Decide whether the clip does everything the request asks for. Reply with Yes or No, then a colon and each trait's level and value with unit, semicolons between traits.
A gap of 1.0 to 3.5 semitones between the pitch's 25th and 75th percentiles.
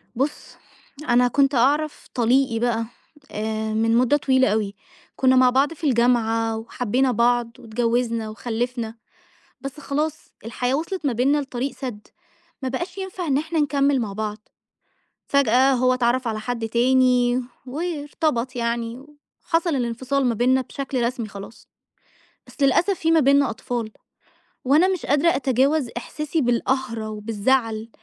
Yes: average, 3.2 semitones